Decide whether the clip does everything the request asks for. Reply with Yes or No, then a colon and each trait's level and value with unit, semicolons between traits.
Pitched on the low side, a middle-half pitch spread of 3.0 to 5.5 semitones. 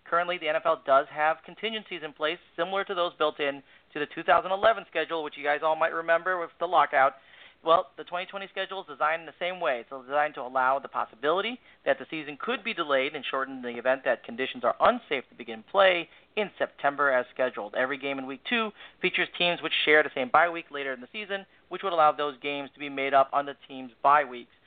No: medium, 155 Hz; average, 4.3 semitones